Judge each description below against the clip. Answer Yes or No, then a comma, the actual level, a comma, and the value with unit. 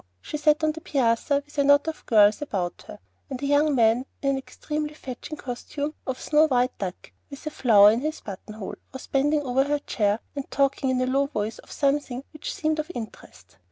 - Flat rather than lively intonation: No, average, 3.7 semitones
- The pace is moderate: No, fast, 215 wpm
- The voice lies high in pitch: Yes, very high, 275 Hz